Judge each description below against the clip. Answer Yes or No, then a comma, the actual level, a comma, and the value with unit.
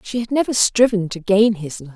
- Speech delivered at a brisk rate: Yes, fast, 245 wpm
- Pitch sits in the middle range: No, high, 210 Hz